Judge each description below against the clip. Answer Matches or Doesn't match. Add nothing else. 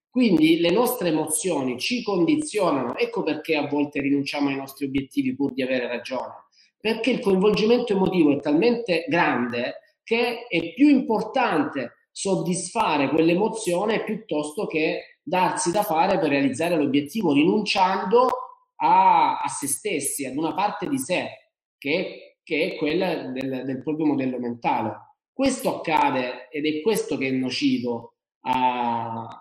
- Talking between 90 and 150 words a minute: Matches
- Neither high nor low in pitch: Matches